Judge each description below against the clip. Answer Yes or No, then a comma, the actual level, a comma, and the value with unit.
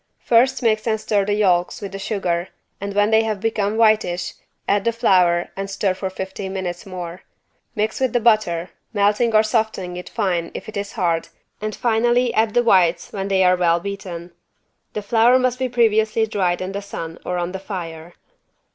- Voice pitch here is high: Yes, high, 200 Hz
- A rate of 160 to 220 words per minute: Yes, average, 190 wpm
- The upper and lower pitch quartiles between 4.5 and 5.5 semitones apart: No, average, 3.4 semitones